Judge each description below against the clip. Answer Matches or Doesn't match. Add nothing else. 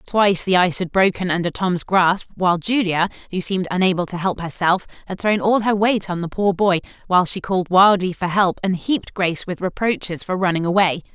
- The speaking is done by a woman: Matches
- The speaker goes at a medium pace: Doesn't match